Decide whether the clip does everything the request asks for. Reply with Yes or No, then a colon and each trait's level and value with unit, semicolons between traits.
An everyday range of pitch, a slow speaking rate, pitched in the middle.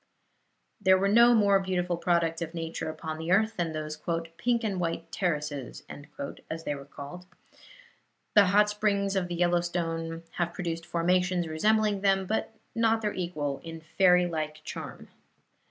No: average, 3.3 semitones; average, 155 wpm; medium, 175 Hz